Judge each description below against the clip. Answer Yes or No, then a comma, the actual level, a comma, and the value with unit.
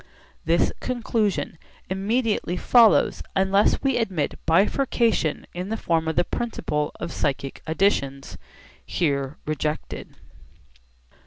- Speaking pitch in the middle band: Yes, medium, 180 Hz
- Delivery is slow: Yes, slow, 100 wpm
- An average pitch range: No, wide, 6.2 semitones